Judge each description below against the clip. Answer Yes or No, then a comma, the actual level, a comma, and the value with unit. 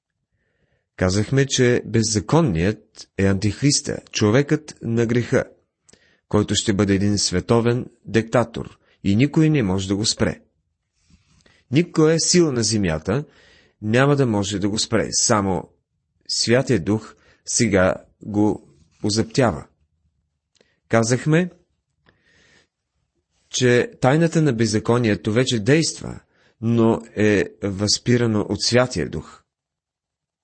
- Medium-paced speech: No, slow, 100 wpm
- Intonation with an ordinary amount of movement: Yes, average, 4.0 semitones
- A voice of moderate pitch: No, low, 110 Hz